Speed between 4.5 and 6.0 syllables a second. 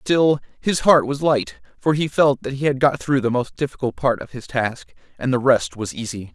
Yes: 5.0 syllables/s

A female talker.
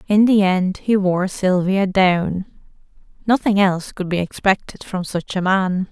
Yes: female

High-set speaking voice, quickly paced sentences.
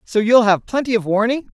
Yes: high, 225 Hz; fast, 235 wpm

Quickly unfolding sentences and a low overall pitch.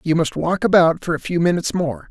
No: fast, 255 wpm; medium, 165 Hz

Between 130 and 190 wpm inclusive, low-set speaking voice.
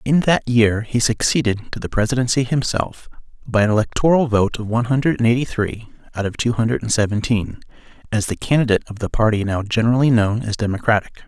Yes: average, 180 wpm; low, 115 Hz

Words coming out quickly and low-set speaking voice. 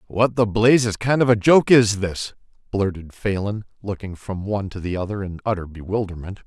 No: average, 185 wpm; low, 105 Hz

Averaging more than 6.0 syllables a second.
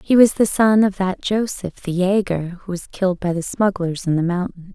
No: 5.0 syllables/s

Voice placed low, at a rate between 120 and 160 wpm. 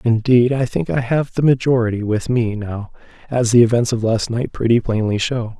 No: low, 115 Hz; fast, 205 wpm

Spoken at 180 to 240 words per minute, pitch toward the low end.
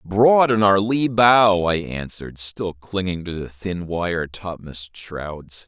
No: average, 160 wpm; very low, 95 Hz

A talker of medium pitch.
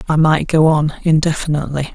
Yes: medium, 155 Hz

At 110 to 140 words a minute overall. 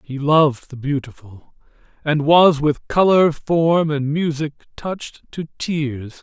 Yes: slow, 135 wpm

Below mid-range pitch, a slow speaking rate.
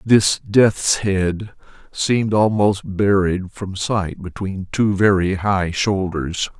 Yes: low, 100 Hz; slow, 120 wpm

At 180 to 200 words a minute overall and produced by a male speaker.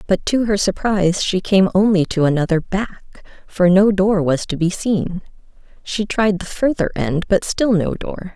No: average, 185 wpm; female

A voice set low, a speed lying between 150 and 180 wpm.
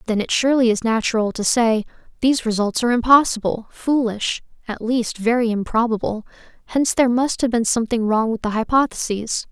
No: high, 230 Hz; average, 165 wpm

